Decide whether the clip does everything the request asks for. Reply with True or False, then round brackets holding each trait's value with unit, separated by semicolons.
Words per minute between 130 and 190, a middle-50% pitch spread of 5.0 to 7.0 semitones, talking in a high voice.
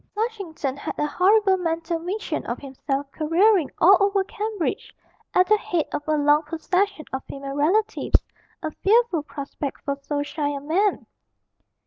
True (150 wpm; 5.5 semitones; 330 Hz)